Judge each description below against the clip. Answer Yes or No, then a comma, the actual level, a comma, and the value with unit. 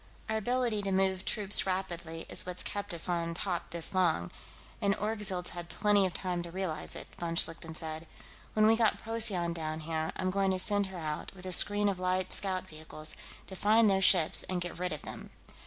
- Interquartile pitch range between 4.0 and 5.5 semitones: No, average, 3.0 semitones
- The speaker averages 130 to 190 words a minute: No, fast, 205 wpm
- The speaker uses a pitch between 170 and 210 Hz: Yes, medium, 185 Hz